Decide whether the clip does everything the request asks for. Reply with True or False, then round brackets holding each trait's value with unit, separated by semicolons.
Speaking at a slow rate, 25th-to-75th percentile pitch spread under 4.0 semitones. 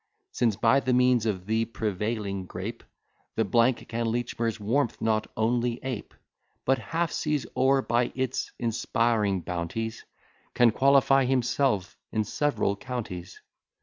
True (125 wpm; 3.1 semitones)